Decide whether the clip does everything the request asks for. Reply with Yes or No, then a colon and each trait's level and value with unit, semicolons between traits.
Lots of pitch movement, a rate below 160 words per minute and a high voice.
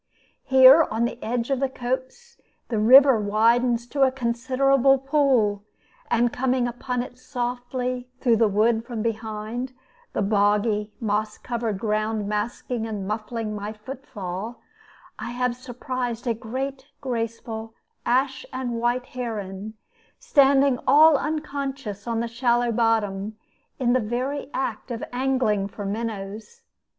No: average, 3.0 semitones; slow, 135 wpm; high, 240 Hz